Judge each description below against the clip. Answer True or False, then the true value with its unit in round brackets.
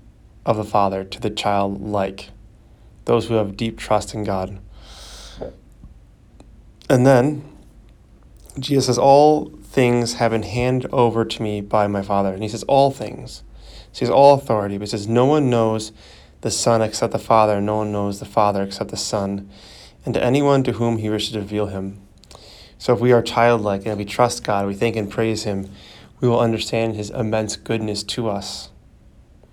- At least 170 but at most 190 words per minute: True (185 wpm)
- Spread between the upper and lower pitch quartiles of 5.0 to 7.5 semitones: False (2.7 semitones)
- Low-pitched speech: True (110 Hz)